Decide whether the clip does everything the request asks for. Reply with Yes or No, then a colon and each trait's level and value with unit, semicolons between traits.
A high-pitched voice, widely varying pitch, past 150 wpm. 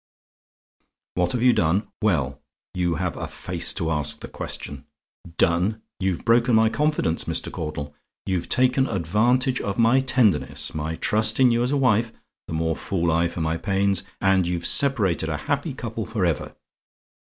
No: very low, 95 Hz; wide, 6.3 semitones; average, 165 wpm